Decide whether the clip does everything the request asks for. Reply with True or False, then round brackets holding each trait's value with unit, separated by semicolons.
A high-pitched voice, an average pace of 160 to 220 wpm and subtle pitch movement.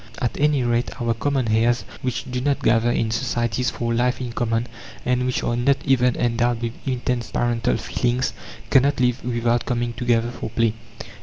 False (120 Hz; 175 wpm; 1.3 semitones)